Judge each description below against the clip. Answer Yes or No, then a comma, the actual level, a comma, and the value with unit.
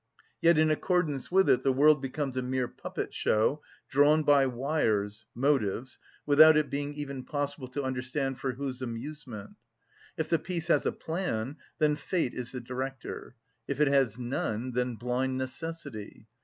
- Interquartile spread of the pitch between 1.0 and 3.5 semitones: Yes, average, 3.2 semitones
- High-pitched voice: No, low, 135 Hz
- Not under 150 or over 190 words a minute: Yes, average, 155 wpm